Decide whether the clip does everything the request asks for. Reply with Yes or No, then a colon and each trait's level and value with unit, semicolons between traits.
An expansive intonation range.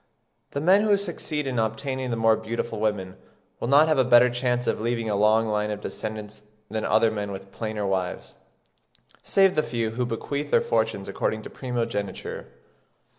No: average, 3.2 semitones